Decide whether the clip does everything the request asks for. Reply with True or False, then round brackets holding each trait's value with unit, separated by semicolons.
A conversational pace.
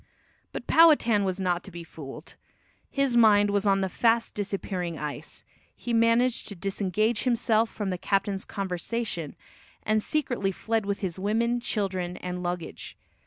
True (150 wpm)